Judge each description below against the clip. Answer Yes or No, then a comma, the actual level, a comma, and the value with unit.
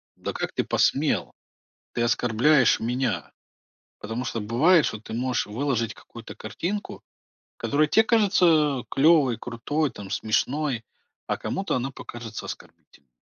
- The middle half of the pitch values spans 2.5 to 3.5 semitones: No, average, 4.9 semitones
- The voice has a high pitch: No, low, 125 Hz